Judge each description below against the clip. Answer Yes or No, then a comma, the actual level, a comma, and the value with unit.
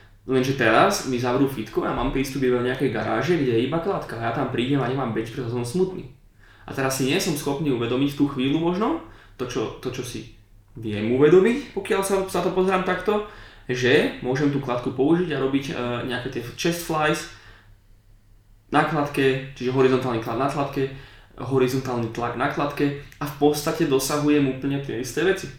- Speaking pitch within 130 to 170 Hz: Yes, low, 135 Hz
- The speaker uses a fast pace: Yes, fast, 185 wpm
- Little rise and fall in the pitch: No, average, 3.6 semitones